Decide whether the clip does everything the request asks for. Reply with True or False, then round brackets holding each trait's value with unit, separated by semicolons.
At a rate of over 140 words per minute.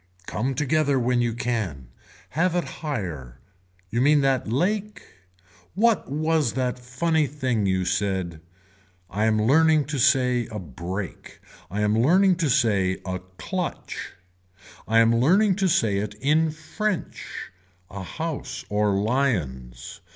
False (135 wpm)